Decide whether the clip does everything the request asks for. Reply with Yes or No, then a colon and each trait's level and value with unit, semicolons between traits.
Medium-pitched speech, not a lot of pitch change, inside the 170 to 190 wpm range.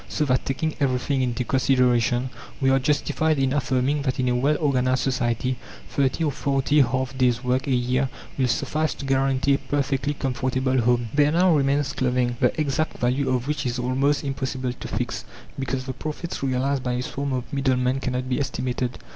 No: low, 130 Hz; narrow, 1.8 semitones; average, 185 wpm